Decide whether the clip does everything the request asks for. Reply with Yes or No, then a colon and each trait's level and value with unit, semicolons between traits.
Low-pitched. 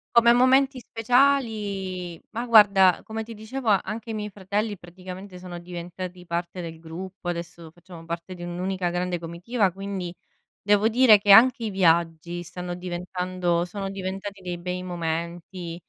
No: medium, 185 Hz